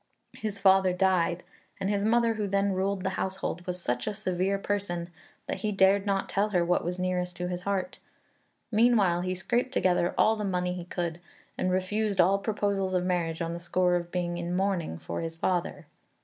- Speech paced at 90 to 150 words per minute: No, average, 195 wpm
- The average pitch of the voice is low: No, medium, 185 Hz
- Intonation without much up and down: Yes, narrow, 2.1 semitones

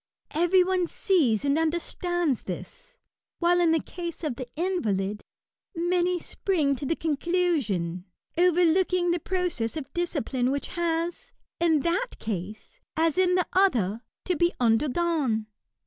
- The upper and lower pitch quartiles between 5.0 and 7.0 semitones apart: Yes, average, 5.3 semitones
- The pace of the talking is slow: Yes, slow, 130 wpm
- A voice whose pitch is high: Yes, very high, 330 Hz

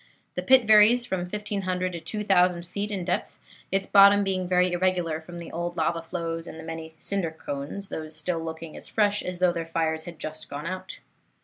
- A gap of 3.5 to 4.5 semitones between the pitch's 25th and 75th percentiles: No, average, 3.0 semitones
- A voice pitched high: No, medium, 180 Hz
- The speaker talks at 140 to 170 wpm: No, average, 200 wpm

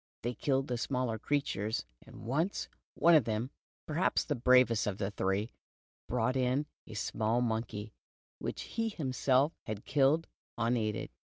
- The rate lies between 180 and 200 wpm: No, average, 145 wpm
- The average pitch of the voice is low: Yes, low, 125 Hz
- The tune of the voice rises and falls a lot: No, average, 3.8 semitones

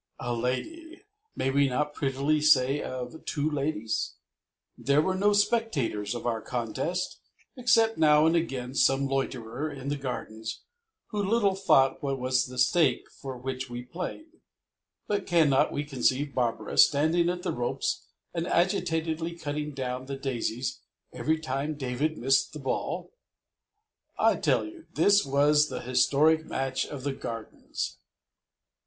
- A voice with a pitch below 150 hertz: Yes, medium, 140 Hz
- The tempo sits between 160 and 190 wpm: No, average, 145 wpm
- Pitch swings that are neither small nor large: Yes, average, 4.1 semitones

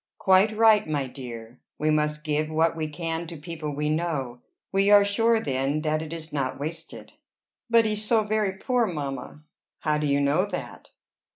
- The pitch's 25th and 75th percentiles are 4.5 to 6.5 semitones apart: Yes, average, 5.2 semitones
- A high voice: No, medium, 155 Hz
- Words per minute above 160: Yes, average, 180 wpm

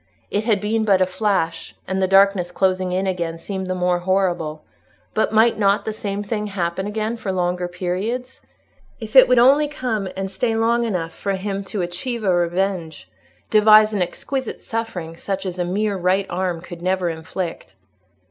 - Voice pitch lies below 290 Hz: Yes, high, 190 Hz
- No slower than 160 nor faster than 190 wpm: Yes, average, 175 wpm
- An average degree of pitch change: Yes, average, 3.3 semitones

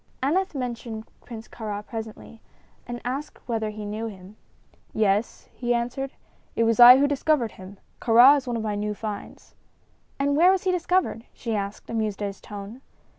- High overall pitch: Yes, high, 230 Hz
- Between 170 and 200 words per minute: Yes, average, 175 wpm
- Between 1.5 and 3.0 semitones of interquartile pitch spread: No, average, 3.9 semitones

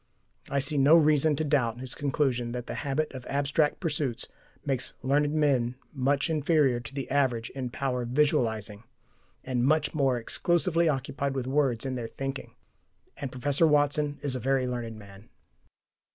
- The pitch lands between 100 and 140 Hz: Yes, low, 135 Hz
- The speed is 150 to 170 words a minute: Yes, average, 165 wpm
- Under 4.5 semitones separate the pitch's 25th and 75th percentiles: Yes, average, 2.9 semitones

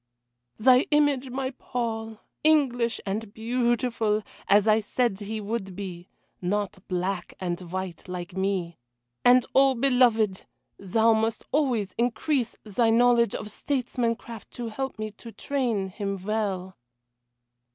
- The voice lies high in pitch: Yes, high, 220 Hz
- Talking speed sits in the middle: No, slow, 125 wpm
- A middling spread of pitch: Yes, average, 3.8 semitones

